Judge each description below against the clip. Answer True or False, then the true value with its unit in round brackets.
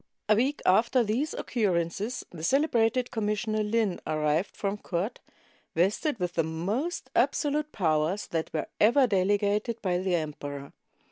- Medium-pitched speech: False (205 Hz)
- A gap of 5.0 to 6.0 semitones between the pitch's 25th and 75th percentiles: True (5.5 semitones)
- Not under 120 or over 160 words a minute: True (140 wpm)